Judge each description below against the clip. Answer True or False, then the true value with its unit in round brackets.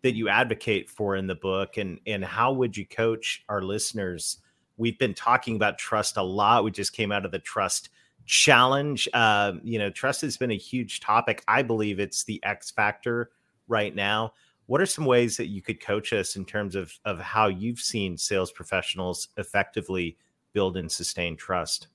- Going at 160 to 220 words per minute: True (190 wpm)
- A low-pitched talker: True (110 Hz)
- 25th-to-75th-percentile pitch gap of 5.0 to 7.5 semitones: False (3.5 semitones)